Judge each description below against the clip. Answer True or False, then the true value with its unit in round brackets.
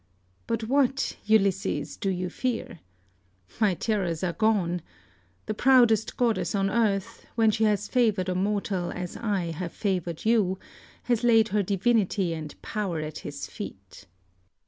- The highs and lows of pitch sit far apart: False (3.6 semitones)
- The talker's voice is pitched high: True (205 Hz)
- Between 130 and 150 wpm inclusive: True (145 wpm)